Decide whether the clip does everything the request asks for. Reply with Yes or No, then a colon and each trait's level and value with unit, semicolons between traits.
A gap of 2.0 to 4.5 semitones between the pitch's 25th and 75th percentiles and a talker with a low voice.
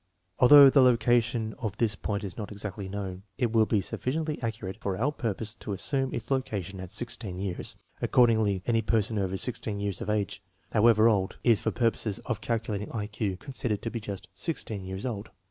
Yes: average, 2.9 semitones; low, 110 Hz